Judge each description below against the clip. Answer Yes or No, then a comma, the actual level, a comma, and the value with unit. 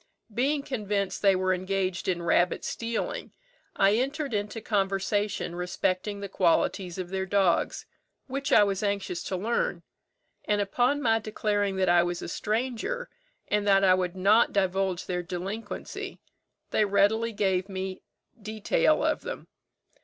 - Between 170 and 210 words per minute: No, average, 145 wpm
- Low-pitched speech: No, high, 200 Hz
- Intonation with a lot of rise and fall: No, average, 2.9 semitones